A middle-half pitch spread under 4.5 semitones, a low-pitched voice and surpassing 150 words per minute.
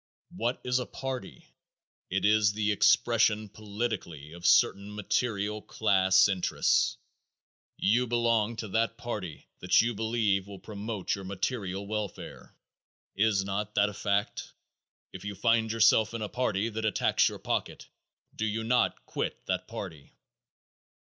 No: narrow, 2.5 semitones; low, 105 Hz; average, 140 wpm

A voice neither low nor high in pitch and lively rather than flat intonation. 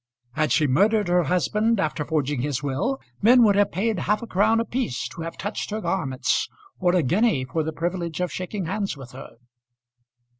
Yes: medium, 180 Hz; wide, 5.8 semitones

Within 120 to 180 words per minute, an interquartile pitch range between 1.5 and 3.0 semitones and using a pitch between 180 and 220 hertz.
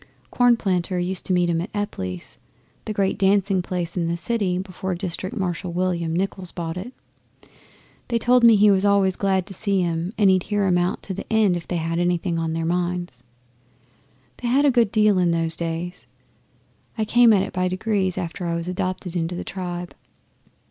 No: average, 195 wpm; narrow, 2.5 semitones; medium, 185 Hz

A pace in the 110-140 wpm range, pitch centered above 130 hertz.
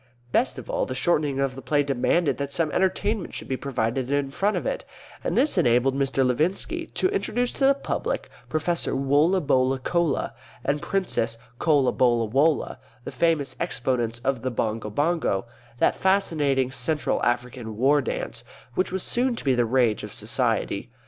No: average, 160 wpm; medium, 140 Hz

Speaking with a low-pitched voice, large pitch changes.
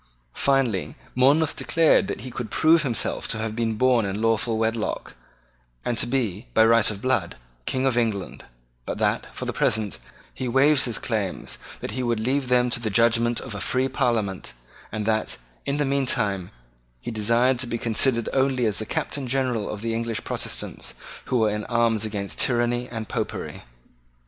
No: low, 115 Hz; average, 2.9 semitones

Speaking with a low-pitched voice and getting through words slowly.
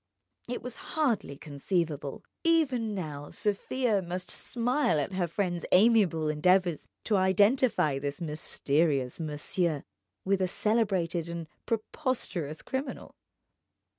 No: medium, 185 Hz; slow, 105 wpm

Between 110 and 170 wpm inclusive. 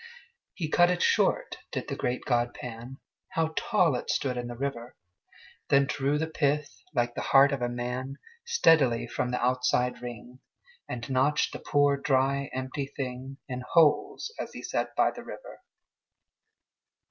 Yes: average, 160 wpm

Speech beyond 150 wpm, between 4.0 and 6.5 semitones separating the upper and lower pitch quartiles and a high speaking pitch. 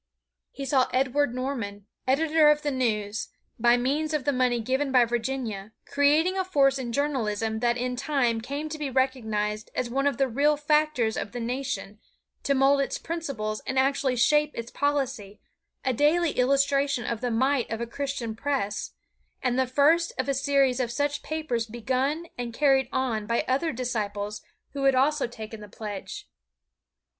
No: average, 170 wpm; average, 3.4 semitones; very high, 260 Hz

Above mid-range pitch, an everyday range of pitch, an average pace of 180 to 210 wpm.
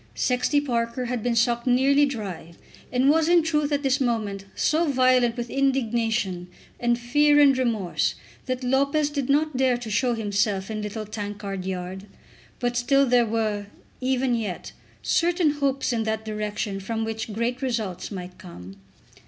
No: high, 240 Hz; average, 4.2 semitones; average, 160 wpm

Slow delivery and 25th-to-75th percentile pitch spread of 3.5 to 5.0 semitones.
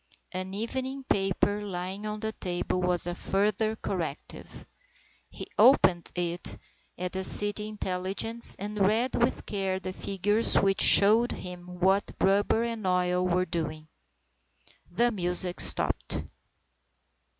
No: slow, 125 wpm; average, 2.9 semitones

